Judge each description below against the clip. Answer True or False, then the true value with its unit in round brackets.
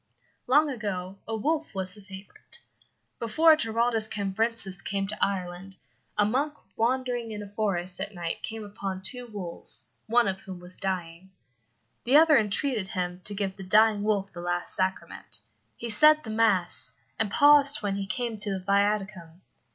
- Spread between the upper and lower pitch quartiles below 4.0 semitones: True (3.5 semitones)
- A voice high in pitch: True (205 Hz)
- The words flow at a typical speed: True (165 wpm)